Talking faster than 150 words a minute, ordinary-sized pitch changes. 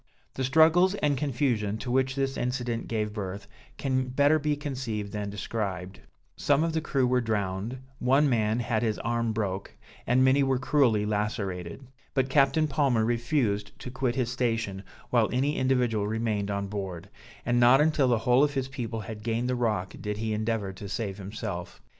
Yes: average, 175 wpm; average, 4.1 semitones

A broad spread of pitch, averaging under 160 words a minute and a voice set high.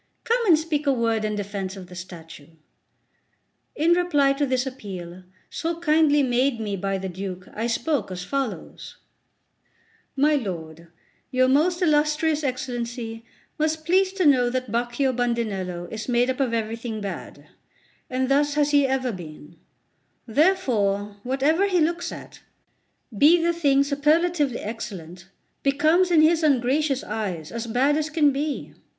Yes: wide, 6.1 semitones; average, 145 wpm; very high, 260 Hz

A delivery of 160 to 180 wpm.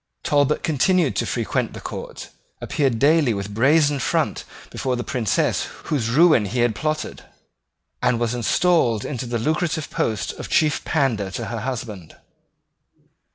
No: average, 145 wpm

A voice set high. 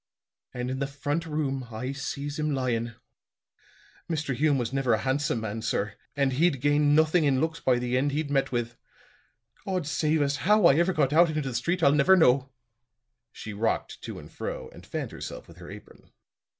No: medium, 140 Hz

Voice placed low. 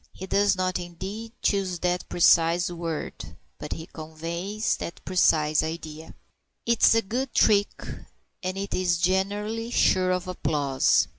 No: medium, 180 Hz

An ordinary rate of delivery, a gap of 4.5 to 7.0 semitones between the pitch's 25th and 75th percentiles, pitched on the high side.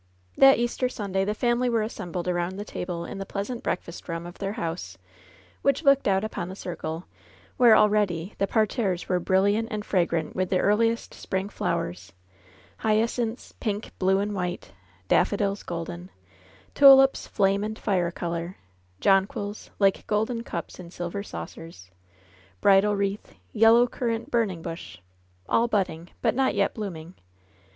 No: average, 155 wpm; average, 4.0 semitones; high, 195 Hz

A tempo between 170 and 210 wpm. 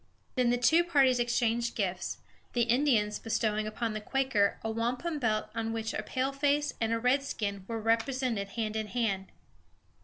No: average, 160 wpm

